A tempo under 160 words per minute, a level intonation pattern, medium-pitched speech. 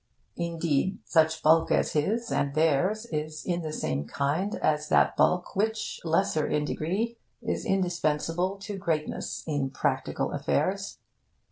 No: slow, 135 wpm; average, 4.2 semitones; medium, 165 Hz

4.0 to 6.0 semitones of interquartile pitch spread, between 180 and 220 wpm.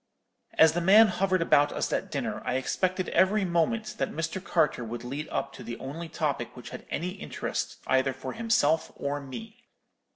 Yes: wide, 5.5 semitones; average, 185 wpm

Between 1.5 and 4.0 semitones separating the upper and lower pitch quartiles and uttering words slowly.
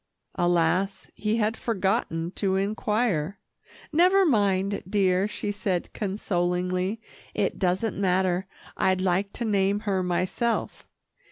Yes: narrow, 2.6 semitones; slow, 110 wpm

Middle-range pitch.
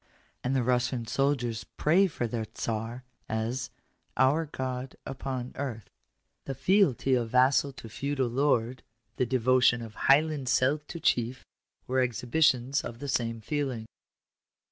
No: low, 130 Hz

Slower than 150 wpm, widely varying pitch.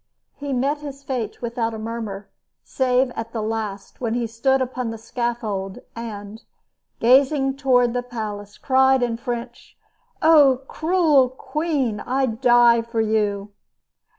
No: slow, 135 wpm; average, 3.0 semitones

